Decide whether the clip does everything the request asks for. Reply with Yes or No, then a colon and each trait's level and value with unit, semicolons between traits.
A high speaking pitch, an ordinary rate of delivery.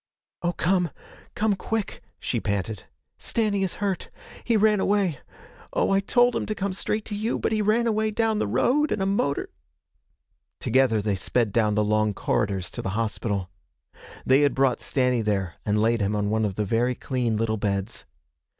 No: low, 130 Hz; average, 185 wpm